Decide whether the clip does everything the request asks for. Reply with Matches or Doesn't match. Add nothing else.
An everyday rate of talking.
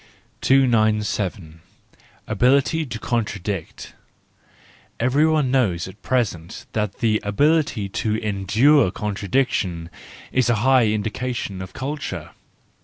Doesn't match